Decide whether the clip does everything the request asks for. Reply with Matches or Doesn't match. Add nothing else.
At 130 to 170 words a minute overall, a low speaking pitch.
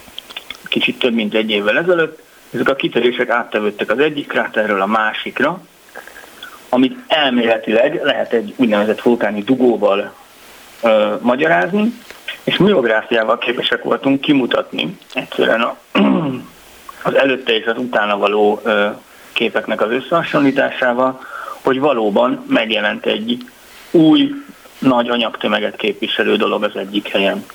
Doesn't match